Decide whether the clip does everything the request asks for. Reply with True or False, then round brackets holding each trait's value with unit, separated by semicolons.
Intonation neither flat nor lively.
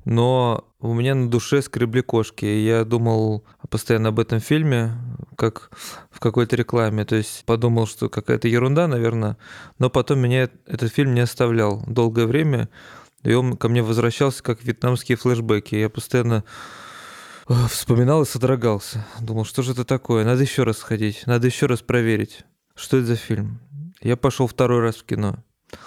False (2.2 semitones)